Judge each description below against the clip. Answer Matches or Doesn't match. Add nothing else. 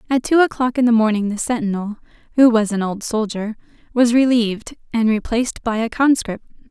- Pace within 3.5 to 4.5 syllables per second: Doesn't match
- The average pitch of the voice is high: Matches